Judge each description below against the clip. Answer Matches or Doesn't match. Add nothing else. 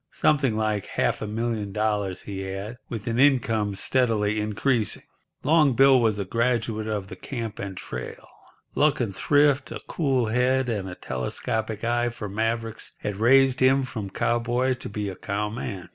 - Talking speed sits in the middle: Matches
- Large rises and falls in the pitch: Doesn't match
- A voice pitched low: Matches